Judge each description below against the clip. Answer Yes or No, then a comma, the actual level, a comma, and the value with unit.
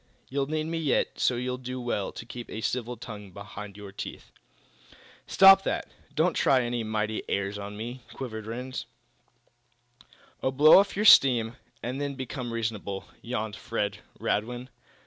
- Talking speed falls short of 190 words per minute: Yes, average, 160 wpm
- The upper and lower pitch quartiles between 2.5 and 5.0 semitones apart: Yes, average, 3.4 semitones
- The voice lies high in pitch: No, low, 120 Hz